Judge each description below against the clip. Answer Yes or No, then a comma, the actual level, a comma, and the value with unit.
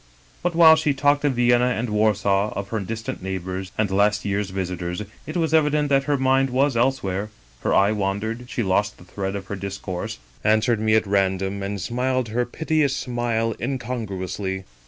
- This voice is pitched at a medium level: No, low, 110 Hz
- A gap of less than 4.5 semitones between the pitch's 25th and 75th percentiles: No, average, 4.8 semitones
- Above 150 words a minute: Yes, average, 180 wpm